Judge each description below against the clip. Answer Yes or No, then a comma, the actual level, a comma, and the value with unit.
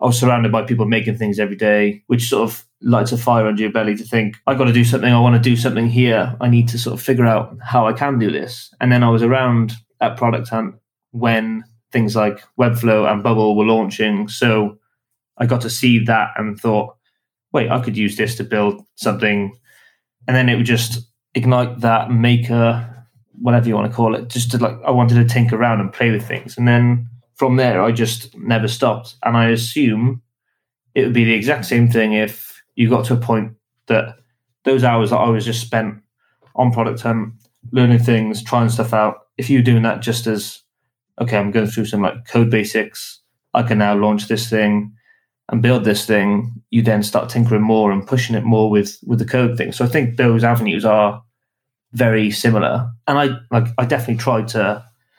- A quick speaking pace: Yes, fast, 210 wpm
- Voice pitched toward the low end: Yes, low, 115 Hz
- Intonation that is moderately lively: No, narrow, 1.8 semitones